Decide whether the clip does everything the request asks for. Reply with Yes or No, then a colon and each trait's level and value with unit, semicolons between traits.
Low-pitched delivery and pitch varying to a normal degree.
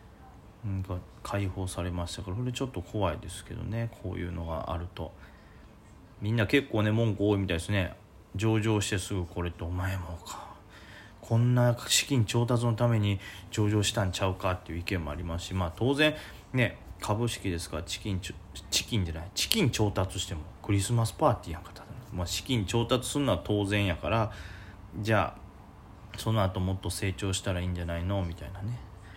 Yes: low, 100 Hz; average, 3.5 semitones